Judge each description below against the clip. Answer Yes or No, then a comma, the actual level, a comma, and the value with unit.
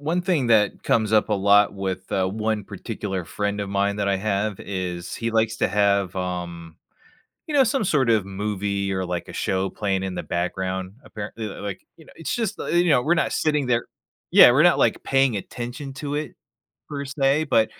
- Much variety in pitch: Yes, wide, 5.8 semitones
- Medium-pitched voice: No, low, 105 Hz